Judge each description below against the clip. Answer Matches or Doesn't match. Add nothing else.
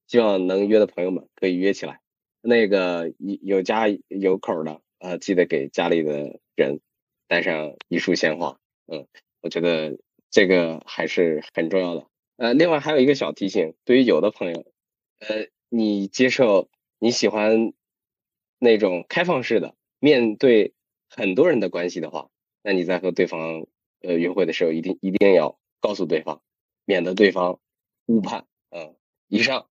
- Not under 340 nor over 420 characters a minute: Doesn't match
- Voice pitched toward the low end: Matches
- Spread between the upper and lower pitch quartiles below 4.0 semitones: Matches